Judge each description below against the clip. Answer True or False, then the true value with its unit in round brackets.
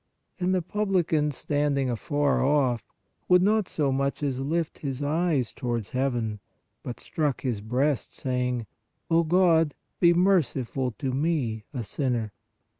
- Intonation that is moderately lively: True (4.6 semitones)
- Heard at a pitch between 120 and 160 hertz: True (140 Hz)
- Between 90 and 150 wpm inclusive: True (140 wpm)